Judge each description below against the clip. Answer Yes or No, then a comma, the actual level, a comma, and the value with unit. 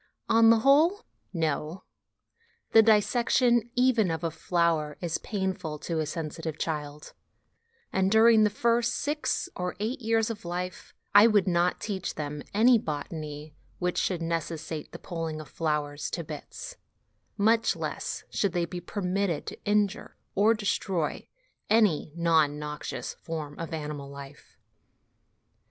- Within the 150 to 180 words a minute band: No, average, 140 wpm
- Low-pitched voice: No, medium, 175 Hz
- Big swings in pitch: Yes, wide, 5.7 semitones